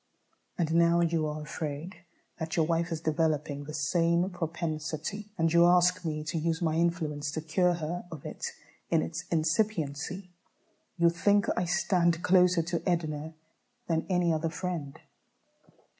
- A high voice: No, medium, 165 Hz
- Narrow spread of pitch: Yes, narrow, 2.1 semitones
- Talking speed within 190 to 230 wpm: No, average, 150 wpm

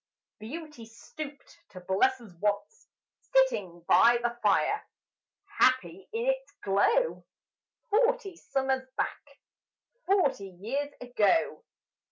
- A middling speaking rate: No, slow, 100 wpm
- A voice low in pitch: No, very high, 260 Hz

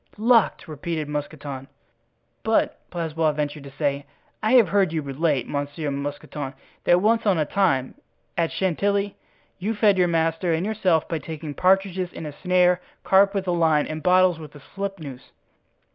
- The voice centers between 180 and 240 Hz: No, medium, 165 Hz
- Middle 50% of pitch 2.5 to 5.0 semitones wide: Yes, average, 4.4 semitones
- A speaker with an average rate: Yes, average, 160 wpm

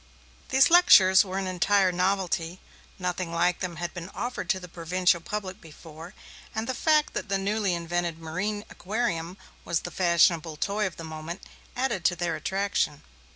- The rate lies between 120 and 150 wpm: No, average, 165 wpm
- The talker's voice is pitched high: No, medium, 180 Hz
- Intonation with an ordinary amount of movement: Yes, average, 3.0 semitones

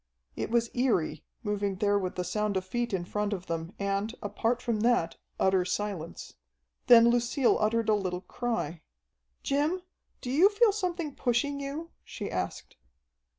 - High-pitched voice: Yes, high, 215 Hz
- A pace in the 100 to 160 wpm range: Yes, average, 155 wpm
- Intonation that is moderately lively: Yes, average, 4.5 semitones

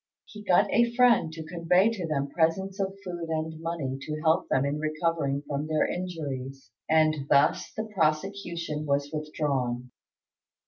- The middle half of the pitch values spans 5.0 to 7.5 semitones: No, average, 3.6 semitones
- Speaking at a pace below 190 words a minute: Yes, average, 150 wpm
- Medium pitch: Yes, medium, 160 Hz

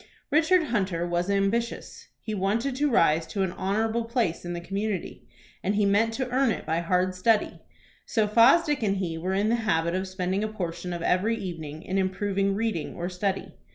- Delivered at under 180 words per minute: No, average, 190 wpm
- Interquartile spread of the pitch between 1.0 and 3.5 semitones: No, average, 4.0 semitones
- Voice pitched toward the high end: Yes, high, 195 Hz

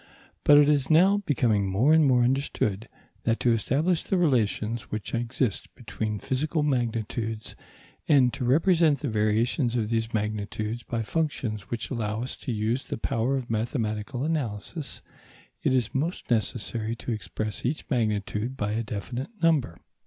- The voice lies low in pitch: Yes, low, 120 Hz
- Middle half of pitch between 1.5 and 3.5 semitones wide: No, average, 4.2 semitones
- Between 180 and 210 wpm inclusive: No, average, 155 wpm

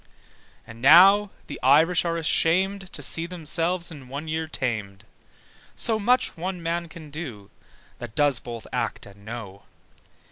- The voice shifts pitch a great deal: Yes, wide, 6.3 semitones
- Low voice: No, medium, 160 Hz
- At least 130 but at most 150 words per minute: Yes, average, 145 wpm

